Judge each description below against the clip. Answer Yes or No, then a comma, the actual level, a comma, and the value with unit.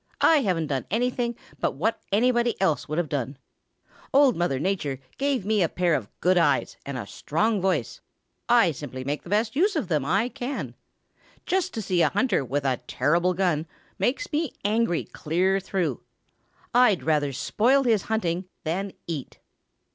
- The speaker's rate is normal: Yes, average, 170 wpm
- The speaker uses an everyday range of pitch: No, wide, 7.5 semitones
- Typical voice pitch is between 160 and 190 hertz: Yes, medium, 185 Hz